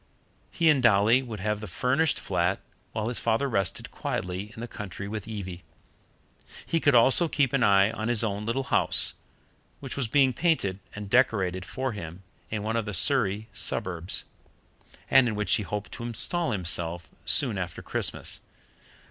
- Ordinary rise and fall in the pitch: Yes, average, 4.5 semitones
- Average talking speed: Yes, average, 170 wpm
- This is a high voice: No, low, 110 Hz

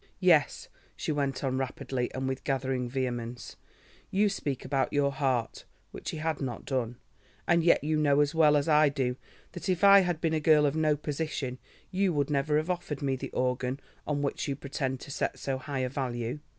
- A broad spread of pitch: No, average, 2.8 semitones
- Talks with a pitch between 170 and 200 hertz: No, medium, 140 Hz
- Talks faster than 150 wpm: Yes, average, 195 wpm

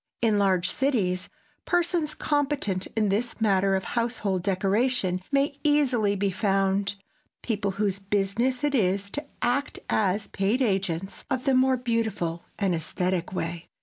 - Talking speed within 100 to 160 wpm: Yes, average, 140 wpm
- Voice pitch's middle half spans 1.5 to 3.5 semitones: No, average, 4.7 semitones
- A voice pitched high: Yes, high, 205 Hz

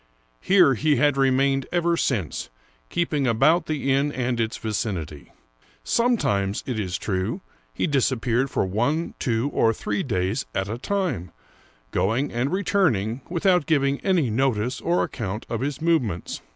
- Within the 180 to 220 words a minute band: No, average, 155 wpm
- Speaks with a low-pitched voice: Yes, low, 130 Hz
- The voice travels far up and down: Yes, wide, 5.9 semitones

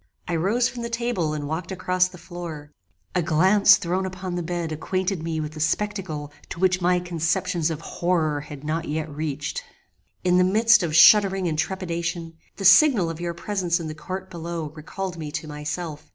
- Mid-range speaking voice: Yes, medium, 175 Hz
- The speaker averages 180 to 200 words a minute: Yes, average, 190 wpm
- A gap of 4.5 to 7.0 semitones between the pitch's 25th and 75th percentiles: No, average, 2.9 semitones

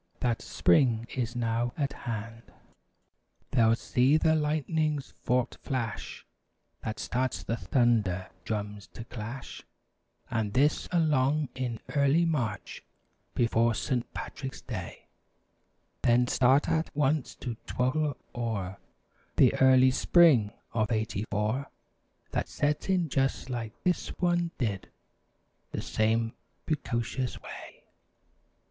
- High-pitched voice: No, low, 125 Hz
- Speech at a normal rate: No, slow, 115 wpm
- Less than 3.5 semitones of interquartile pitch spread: No, average, 4.2 semitones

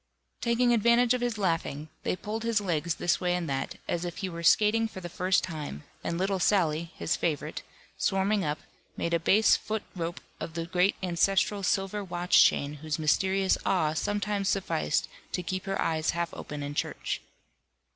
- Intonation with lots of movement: No, average, 3.6 semitones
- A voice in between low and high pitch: Yes, medium, 180 Hz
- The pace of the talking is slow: No, average, 180 wpm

